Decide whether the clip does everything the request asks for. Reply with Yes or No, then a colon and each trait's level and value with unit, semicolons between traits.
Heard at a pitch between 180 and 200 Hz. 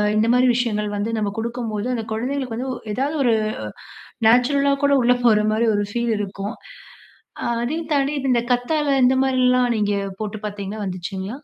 No: high, 235 Hz